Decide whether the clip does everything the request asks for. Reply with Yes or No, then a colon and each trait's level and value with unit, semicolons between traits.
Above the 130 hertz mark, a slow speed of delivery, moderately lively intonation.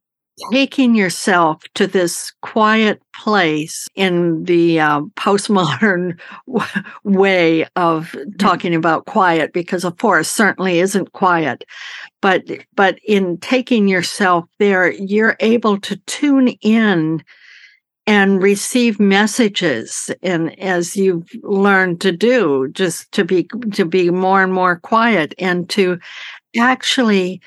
Yes: high, 190 Hz; slow, 120 wpm; average, 3.3 semitones